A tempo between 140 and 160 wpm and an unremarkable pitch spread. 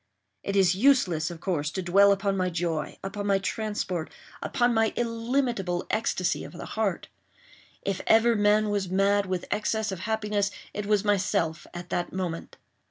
Yes: average, 150 wpm; average, 3.1 semitones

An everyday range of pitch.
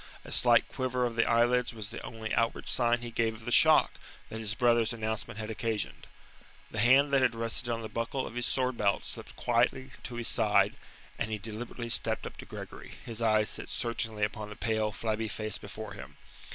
No: narrow, 1.7 semitones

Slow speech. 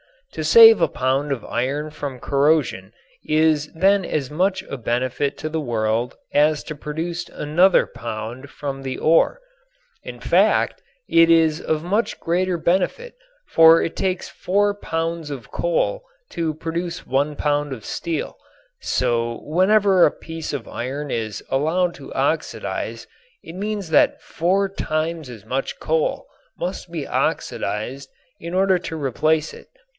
No: average, 145 wpm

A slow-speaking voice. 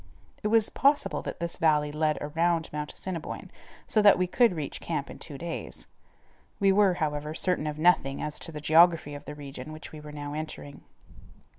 No: average, 190 wpm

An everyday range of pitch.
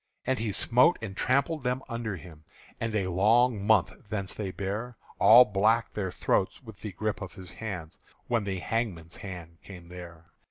Yes: average, 3.9 semitones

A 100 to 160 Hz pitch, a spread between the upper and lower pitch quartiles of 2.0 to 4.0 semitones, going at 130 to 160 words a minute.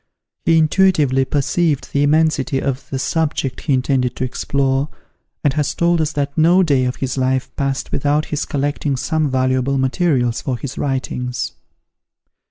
Yes: medium, 140 Hz; average, 2.8 semitones; average, 155 wpm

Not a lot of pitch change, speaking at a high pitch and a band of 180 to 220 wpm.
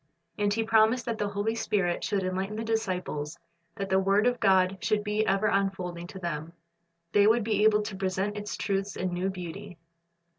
Yes: narrow, 2.3 semitones; high, 200 Hz; average, 190 wpm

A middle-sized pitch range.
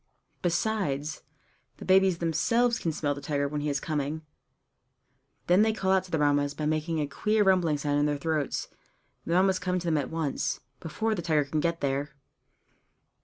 Yes: average, 4.0 semitones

